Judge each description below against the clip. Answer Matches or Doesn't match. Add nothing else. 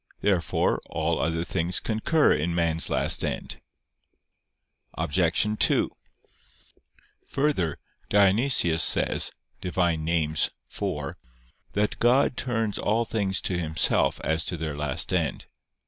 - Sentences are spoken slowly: Matches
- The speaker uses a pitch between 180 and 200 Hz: Doesn't match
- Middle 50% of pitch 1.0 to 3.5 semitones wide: Doesn't match